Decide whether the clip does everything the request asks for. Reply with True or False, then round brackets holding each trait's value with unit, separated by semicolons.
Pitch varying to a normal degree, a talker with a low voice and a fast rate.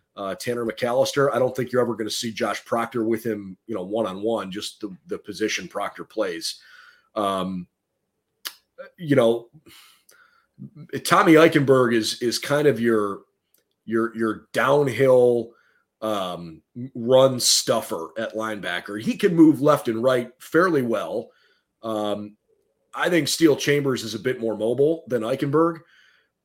False (4.4 semitones; 120 Hz; 145 wpm)